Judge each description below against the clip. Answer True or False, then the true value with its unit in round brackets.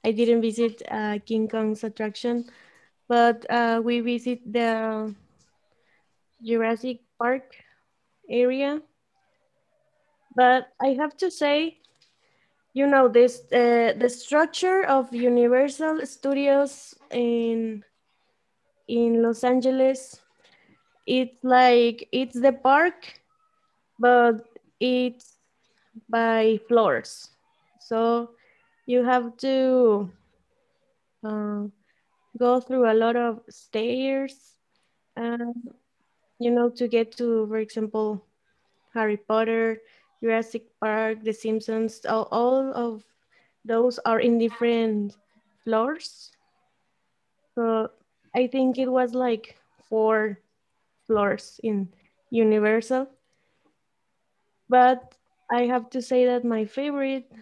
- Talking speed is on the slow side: True (95 wpm)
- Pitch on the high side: True (240 Hz)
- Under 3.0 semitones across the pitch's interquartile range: True (2.5 semitones)